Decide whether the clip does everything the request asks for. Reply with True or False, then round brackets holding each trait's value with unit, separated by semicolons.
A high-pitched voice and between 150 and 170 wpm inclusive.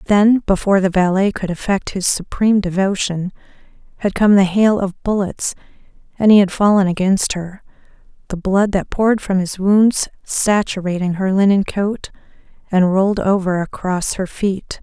True (195 Hz; 155 wpm)